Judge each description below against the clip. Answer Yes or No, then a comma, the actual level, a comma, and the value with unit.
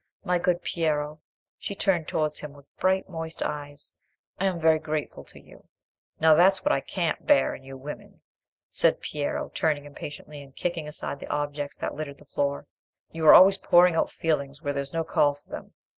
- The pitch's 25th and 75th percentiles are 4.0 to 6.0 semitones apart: No, average, 2.9 semitones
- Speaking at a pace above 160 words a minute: Yes, average, 180 wpm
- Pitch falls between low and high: Yes, medium, 155 Hz